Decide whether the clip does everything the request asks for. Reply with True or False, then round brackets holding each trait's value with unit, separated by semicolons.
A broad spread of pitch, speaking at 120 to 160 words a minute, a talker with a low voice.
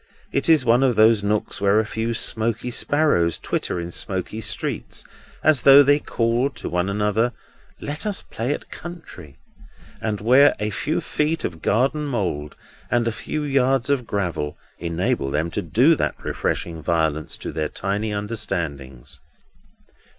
True (7.2 semitones; 155 wpm; 110 Hz)